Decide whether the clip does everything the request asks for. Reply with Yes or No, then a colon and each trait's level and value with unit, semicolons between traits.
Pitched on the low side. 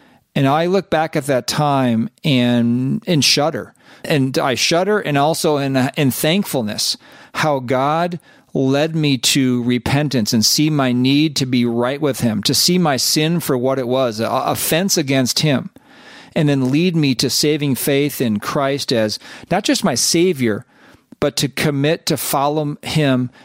No: medium, 145 Hz